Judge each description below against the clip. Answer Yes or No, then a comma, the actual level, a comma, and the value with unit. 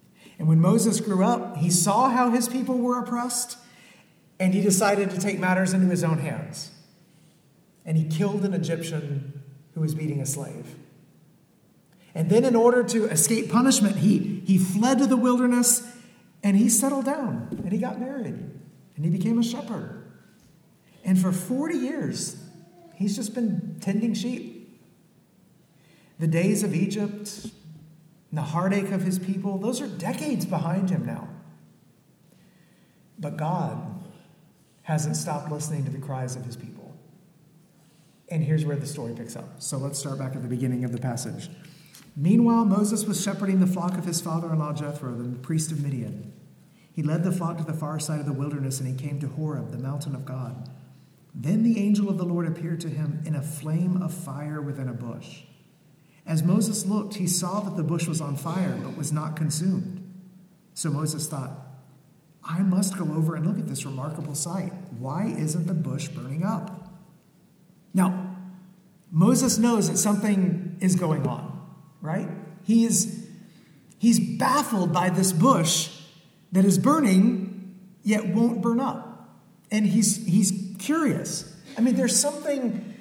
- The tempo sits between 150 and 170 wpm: Yes, average, 165 wpm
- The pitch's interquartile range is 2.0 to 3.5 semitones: No, average, 4.4 semitones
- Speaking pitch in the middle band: Yes, medium, 180 Hz